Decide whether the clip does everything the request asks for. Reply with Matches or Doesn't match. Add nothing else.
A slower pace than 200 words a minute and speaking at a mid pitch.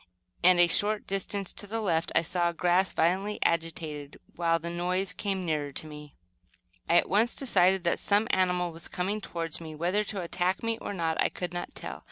Doesn't match